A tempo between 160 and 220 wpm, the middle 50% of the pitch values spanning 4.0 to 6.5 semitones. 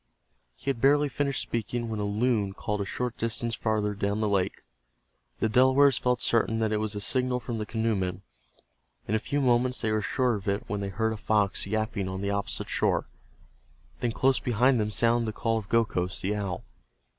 No: average, 200 wpm; average, 3.1 semitones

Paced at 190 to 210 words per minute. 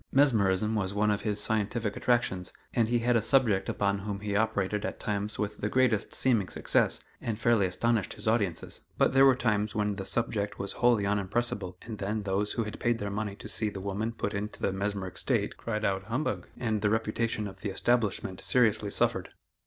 Yes: average, 200 wpm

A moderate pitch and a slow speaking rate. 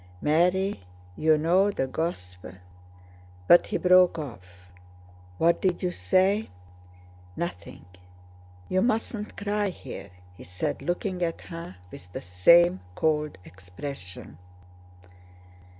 Yes: medium, 165 Hz; slow, 105 wpm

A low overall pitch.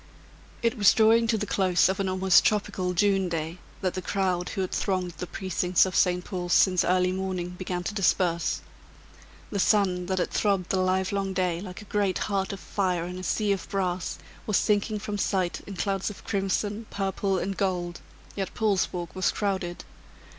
No: high, 190 Hz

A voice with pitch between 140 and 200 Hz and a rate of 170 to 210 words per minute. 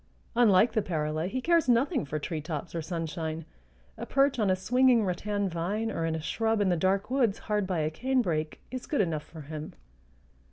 Yes: high, 190 Hz; average, 195 wpm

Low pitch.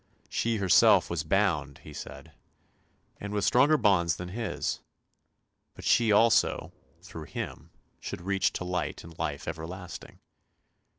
Yes: very low, 90 Hz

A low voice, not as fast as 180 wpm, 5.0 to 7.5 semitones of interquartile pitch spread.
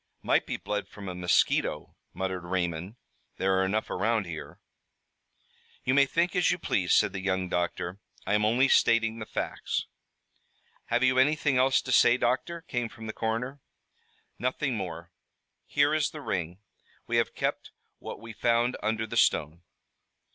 Yes: low, 110 Hz; average, 160 wpm; wide, 5.5 semitones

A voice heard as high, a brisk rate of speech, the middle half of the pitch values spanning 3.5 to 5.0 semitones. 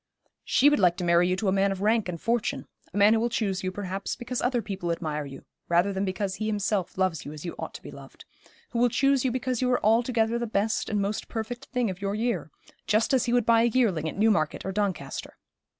Yes: high, 210 Hz; fast, 250 wpm; average, 4.1 semitones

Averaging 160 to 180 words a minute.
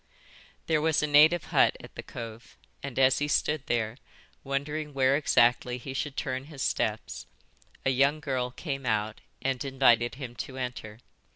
Yes: average, 165 wpm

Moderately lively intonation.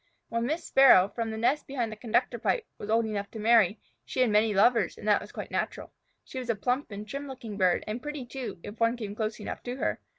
Yes: average, 3.0 semitones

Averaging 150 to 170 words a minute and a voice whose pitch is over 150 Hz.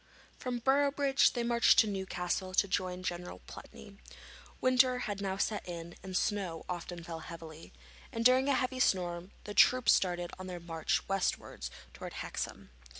Yes: average, 155 wpm; high, 190 Hz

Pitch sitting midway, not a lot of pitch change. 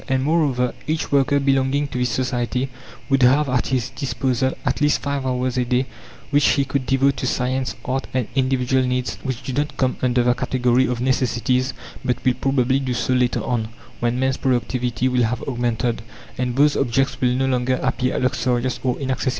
No: low, 130 Hz; narrow, 1.3 semitones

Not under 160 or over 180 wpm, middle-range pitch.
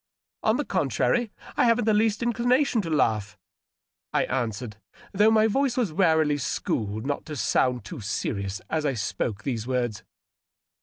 Yes: average, 165 wpm; medium, 150 Hz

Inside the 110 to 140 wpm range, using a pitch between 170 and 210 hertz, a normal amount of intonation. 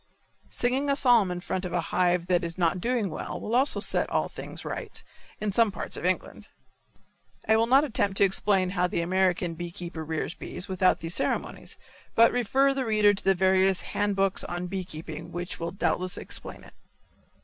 No: average, 195 wpm; high, 190 Hz; average, 3.4 semitones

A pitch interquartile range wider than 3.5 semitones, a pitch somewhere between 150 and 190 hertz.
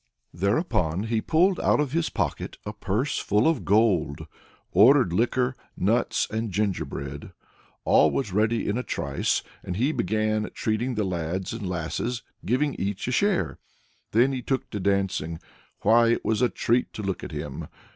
No: average, 4.7 semitones; low, 110 Hz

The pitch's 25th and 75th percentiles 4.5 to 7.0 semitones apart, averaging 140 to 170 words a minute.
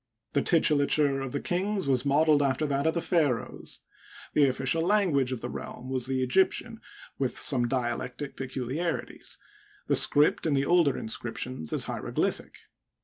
No: average, 3.8 semitones; average, 150 wpm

